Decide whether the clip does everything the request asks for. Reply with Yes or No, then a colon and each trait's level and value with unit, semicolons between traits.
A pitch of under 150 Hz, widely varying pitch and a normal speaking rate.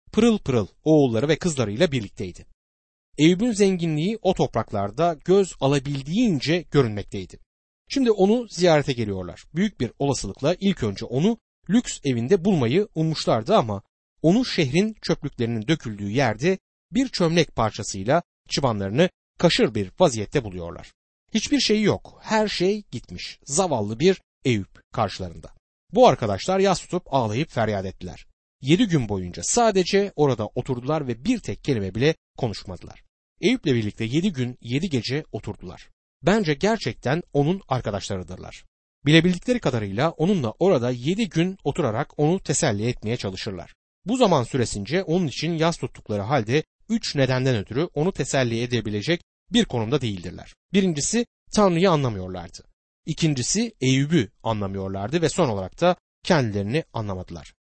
Yes: medium, 140 Hz; wide, 8.7 semitones; average, 125 wpm